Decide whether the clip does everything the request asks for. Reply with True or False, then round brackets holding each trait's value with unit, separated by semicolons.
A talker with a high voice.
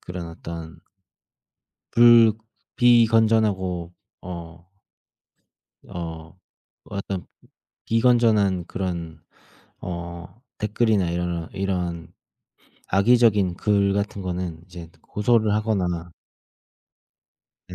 False (95 Hz)